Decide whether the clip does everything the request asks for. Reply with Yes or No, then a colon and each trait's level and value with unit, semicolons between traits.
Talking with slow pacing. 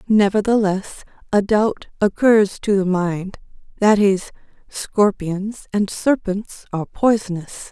Yes: slow, 100 wpm